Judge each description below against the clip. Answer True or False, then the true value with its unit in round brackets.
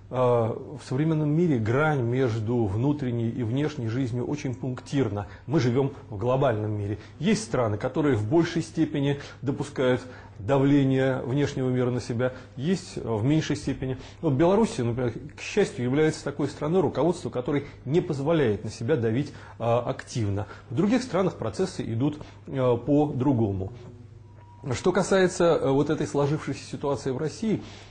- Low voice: True (130 Hz)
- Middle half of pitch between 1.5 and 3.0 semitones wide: False (4.1 semitones)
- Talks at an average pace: True (135 wpm)